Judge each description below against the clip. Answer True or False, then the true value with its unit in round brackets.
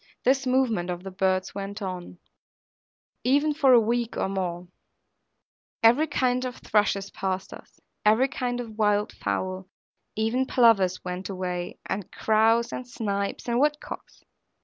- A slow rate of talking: False (145 wpm)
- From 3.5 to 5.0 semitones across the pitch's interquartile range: True (4.6 semitones)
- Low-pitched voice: False (215 Hz)